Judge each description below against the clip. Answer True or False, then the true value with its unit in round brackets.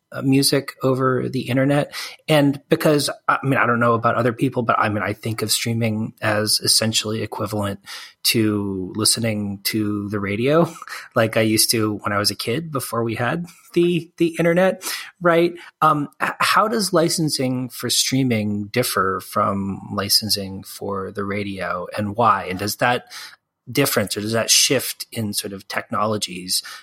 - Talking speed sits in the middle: True (160 wpm)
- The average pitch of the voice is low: True (115 Hz)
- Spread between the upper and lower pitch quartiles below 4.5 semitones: False (4.8 semitones)